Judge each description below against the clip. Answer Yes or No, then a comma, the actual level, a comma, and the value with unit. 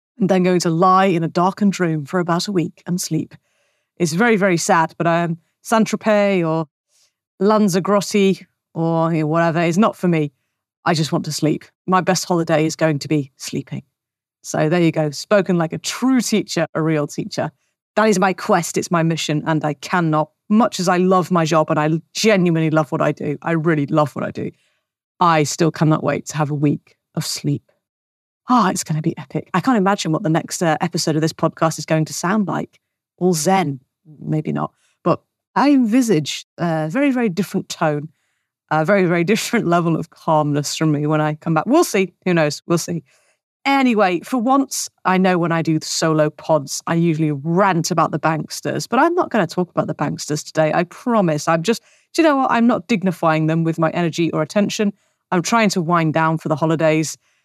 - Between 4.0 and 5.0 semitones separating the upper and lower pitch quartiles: No, average, 3.5 semitones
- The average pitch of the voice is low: No, medium, 165 Hz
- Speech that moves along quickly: Yes, fast, 210 wpm